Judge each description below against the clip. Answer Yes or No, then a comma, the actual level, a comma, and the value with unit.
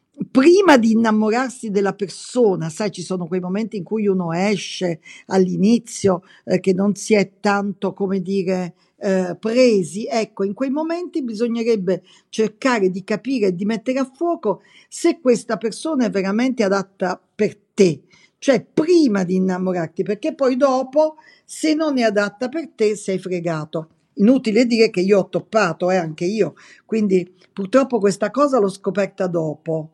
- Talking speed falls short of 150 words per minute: No, average, 155 wpm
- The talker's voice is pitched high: Yes, high, 200 Hz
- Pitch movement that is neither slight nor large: Yes, average, 3.9 semitones